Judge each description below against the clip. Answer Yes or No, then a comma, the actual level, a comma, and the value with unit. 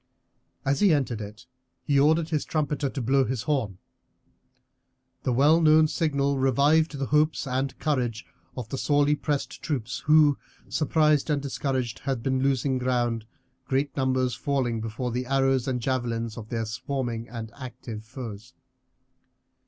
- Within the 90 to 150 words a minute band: Yes, average, 145 wpm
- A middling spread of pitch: Yes, average, 3.2 semitones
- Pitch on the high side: No, low, 135 Hz